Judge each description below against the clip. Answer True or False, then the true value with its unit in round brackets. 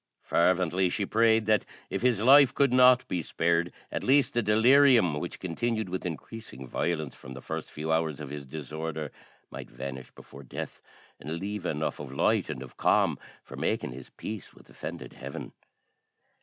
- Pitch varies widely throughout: True (6.9 semitones)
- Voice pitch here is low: True (85 Hz)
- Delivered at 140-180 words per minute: True (170 wpm)